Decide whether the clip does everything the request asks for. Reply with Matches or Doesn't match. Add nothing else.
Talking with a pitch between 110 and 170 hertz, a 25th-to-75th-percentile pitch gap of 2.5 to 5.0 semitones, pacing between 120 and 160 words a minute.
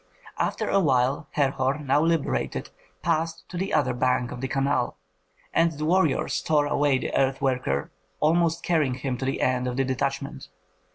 Doesn't match